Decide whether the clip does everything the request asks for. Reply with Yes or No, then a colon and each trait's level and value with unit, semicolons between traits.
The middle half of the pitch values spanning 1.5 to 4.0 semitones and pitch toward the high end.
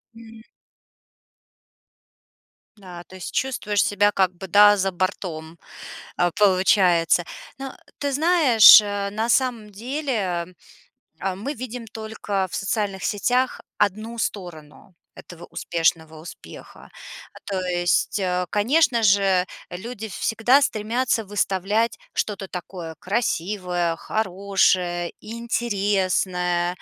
Yes: average, 3.7 semitones; high, 200 Hz